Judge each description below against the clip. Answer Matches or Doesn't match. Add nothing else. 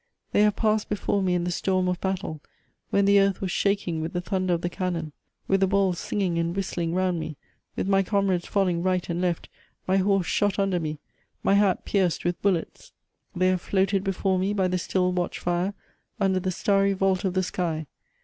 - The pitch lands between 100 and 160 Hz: Doesn't match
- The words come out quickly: Matches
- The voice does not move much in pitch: Matches